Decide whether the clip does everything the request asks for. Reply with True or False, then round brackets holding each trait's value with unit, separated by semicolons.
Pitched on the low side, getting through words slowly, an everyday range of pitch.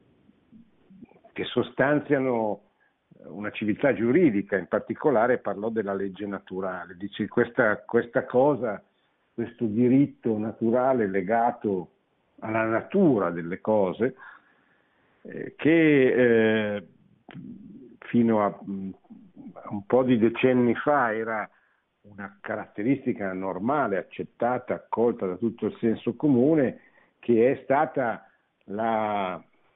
True (110 Hz; 95 wpm; 3.4 semitones)